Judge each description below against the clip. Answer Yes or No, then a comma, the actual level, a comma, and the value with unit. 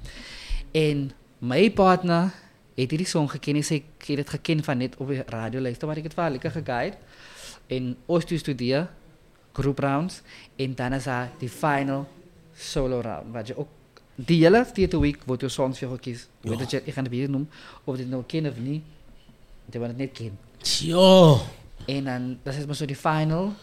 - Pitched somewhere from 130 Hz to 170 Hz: Yes, medium, 140 Hz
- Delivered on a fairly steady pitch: No, average, 3.7 semitones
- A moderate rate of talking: Yes, average, 185 wpm